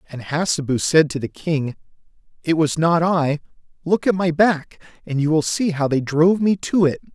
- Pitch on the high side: No, medium, 160 Hz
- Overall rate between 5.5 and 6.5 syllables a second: No, 4.9 syllables/s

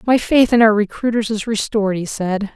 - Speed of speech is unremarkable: No, fast, 210 wpm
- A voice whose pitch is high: Yes, high, 215 Hz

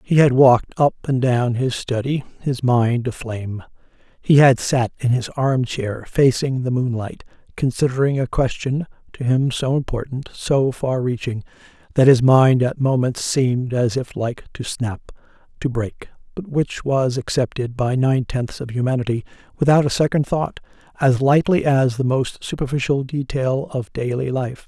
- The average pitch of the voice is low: Yes, low, 130 Hz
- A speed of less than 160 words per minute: No, average, 165 wpm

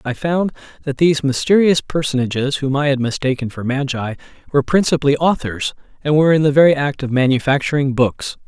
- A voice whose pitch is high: No, medium, 140 Hz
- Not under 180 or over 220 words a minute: No, average, 170 wpm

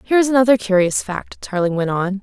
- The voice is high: Yes, high, 210 Hz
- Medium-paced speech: No, fast, 215 wpm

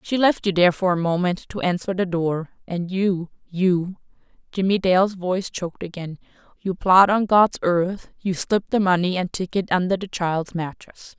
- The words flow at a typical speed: Yes, average, 160 wpm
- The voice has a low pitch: No, medium, 185 Hz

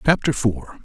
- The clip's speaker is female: No, male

